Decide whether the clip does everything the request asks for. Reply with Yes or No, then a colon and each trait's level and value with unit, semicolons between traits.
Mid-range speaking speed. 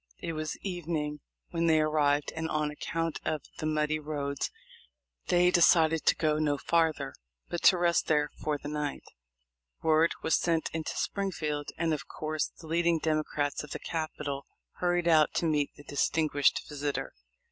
Yes: average, 160 wpm